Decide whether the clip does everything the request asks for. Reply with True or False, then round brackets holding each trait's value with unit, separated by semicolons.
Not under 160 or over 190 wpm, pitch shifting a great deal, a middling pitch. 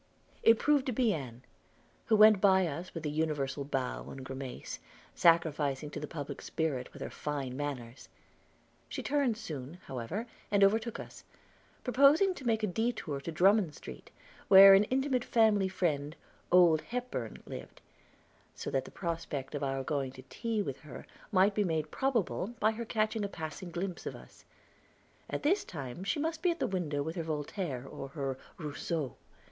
True (175 wpm; 7.4 semitones; 170 Hz)